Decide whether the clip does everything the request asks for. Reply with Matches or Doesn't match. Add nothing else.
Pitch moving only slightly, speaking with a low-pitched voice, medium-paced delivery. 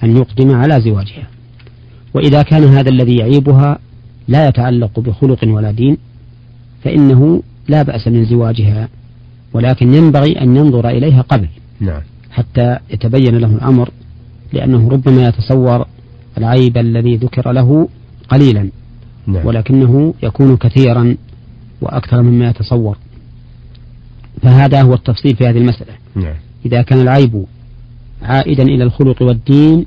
Matches